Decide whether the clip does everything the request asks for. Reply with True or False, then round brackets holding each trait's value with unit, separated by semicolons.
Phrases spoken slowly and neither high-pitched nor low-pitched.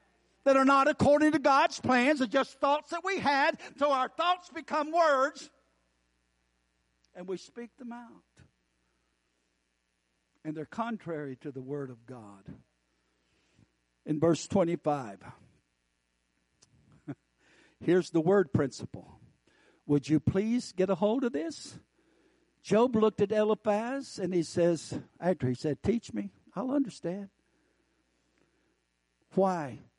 True (120 wpm; 170 Hz)